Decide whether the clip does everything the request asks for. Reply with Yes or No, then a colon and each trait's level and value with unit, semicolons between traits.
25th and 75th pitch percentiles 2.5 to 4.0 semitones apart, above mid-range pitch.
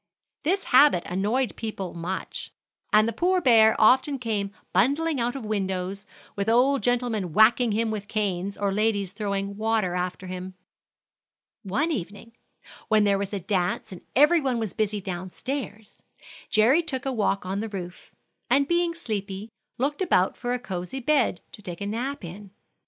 No: average, 4.6 semitones; high, 215 Hz